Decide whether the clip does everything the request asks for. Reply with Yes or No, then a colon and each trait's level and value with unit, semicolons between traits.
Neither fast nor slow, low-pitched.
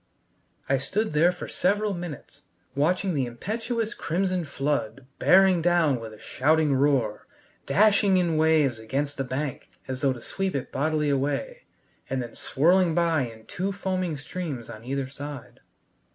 No: average, 150 wpm; medium, 150 Hz